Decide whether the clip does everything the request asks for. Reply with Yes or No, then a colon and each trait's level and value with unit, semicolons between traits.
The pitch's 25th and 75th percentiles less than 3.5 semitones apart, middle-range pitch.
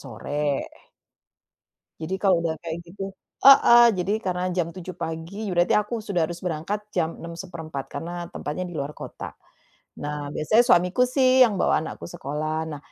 No: average, 3.8 semitones; medium, 170 Hz